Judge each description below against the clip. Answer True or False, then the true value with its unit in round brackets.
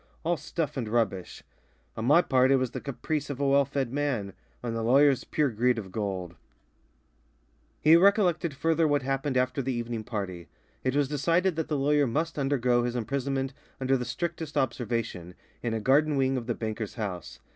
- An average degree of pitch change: True (3.9 semitones)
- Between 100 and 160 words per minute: False (185 wpm)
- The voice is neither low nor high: False (130 Hz)